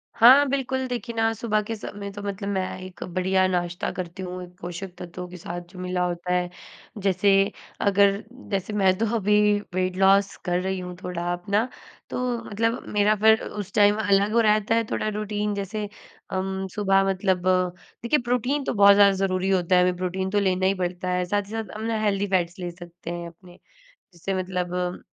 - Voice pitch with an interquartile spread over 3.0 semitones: No, narrow, 2.5 semitones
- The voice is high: Yes, high, 195 Hz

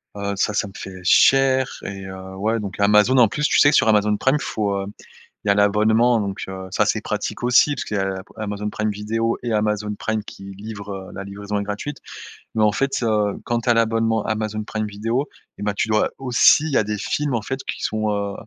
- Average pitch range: No, narrow, 2.1 semitones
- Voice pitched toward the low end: Yes, low, 105 Hz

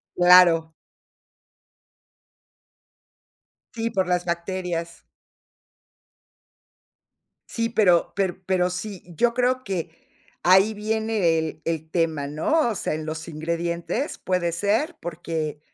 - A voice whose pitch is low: No, medium, 180 Hz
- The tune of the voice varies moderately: Yes, average, 4.0 semitones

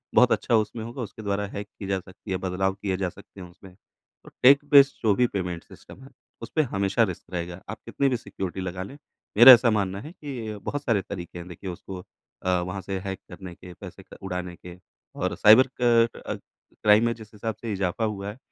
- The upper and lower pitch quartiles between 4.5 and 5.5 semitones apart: No, average, 3.8 semitones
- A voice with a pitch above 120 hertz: No, low, 100 Hz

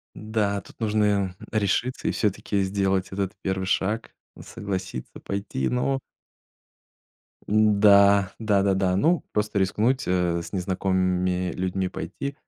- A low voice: Yes, low, 100 Hz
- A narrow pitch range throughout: Yes, narrow, 2.1 semitones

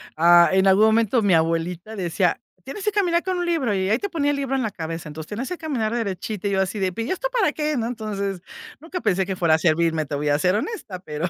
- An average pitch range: No, wide, 7.7 semitones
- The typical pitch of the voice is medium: No, high, 205 Hz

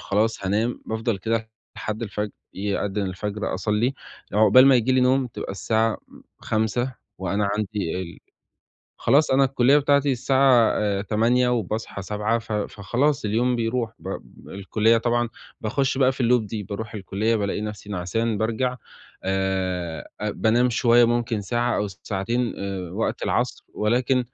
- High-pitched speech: No, low, 110 Hz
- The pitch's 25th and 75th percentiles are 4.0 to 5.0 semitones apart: No, average, 3.2 semitones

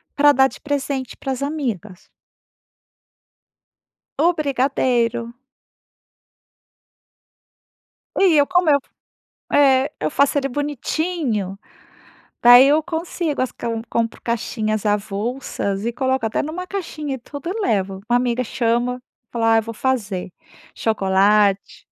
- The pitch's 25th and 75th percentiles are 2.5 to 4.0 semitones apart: No, average, 4.6 semitones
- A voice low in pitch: No, very high, 250 Hz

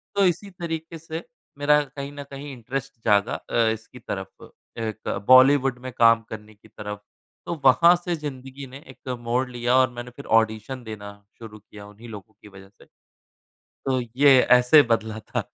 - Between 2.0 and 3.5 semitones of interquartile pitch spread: No, average, 4.4 semitones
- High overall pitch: No, low, 125 Hz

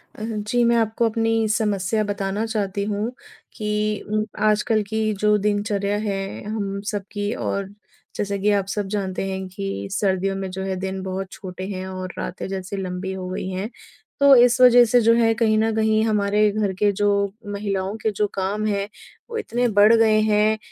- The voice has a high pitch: Yes, high, 205 Hz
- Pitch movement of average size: No, narrow, 2.1 semitones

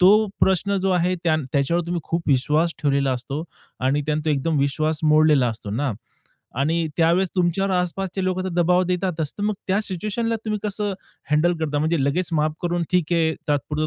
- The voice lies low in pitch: No, medium, 165 Hz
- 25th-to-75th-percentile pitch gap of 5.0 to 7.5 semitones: No, average, 3.5 semitones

